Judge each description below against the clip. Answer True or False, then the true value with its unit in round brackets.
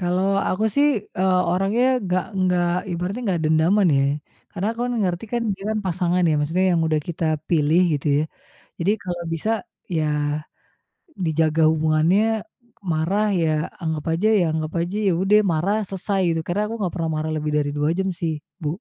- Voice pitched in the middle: True (175 Hz)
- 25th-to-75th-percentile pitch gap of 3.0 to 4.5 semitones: True (3.3 semitones)